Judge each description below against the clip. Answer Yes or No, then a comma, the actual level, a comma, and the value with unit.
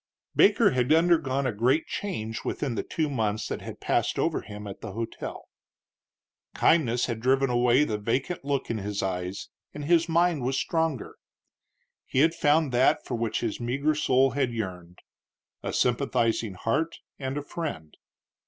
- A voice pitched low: Yes, low, 130 Hz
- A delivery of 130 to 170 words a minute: Yes, average, 160 wpm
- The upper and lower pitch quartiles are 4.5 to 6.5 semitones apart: Yes, average, 4.9 semitones